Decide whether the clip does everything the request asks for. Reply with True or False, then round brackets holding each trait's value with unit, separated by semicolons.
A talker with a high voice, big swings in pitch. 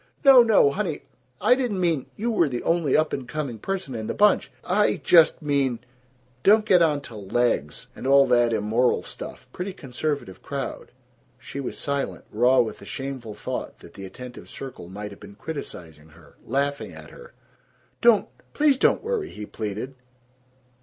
False (140 Hz; 7.9 semitones)